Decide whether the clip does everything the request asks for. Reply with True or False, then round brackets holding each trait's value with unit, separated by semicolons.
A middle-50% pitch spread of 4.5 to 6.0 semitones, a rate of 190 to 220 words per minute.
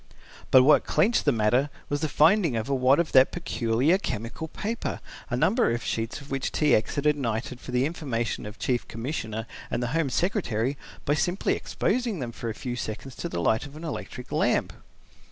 True (5.1 semitones; 205 wpm)